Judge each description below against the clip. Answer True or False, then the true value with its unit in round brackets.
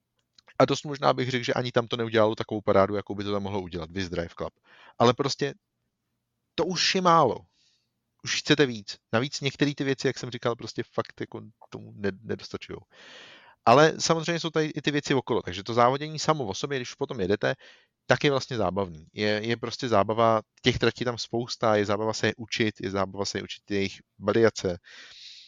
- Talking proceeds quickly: True (195 wpm)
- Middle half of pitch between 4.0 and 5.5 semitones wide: True (4.7 semitones)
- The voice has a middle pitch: False (115 Hz)